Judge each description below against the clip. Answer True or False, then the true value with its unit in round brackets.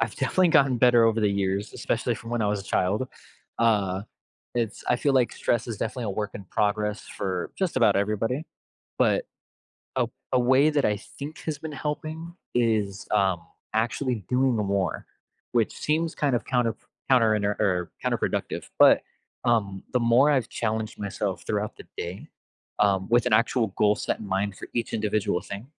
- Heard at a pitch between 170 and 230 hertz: False (110 Hz)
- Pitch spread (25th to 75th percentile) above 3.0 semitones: True (3.7 semitones)